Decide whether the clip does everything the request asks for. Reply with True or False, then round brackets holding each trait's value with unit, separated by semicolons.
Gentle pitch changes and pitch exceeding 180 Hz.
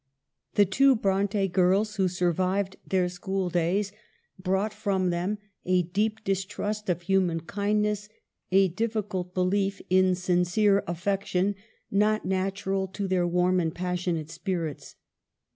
True (2.1 semitones; 190 Hz)